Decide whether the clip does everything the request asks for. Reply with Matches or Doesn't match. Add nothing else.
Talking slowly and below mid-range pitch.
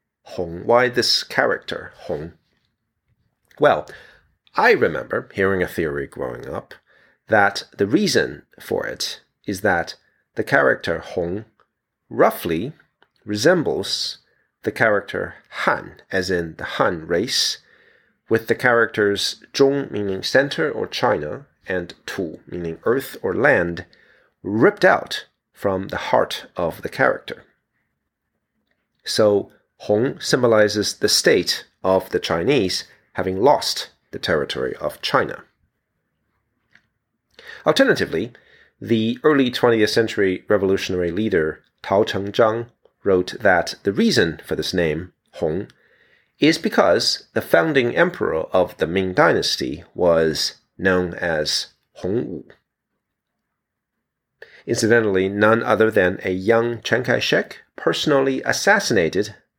Matches